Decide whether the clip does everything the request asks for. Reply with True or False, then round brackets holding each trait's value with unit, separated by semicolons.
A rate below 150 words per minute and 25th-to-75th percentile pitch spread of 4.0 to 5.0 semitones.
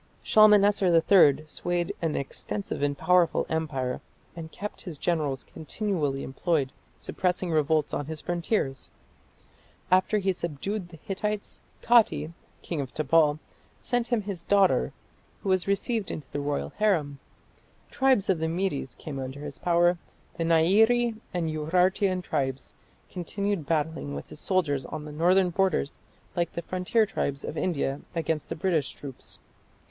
True (140 wpm; 4.5 semitones)